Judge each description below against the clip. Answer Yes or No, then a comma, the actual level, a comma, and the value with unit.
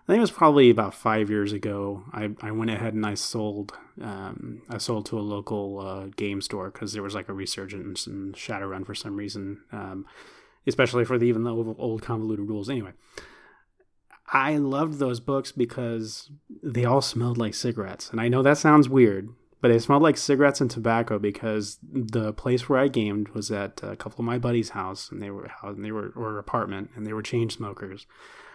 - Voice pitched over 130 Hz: No, low, 110 Hz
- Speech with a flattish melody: No, average, 3.2 semitones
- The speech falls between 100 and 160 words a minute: No, fast, 205 wpm